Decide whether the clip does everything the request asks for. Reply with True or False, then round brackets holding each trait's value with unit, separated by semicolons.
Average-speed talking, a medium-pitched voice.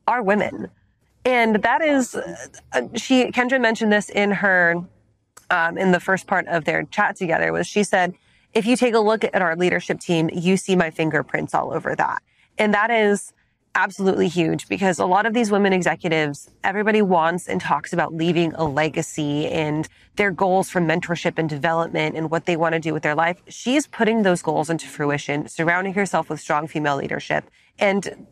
True (185 wpm; 180 Hz)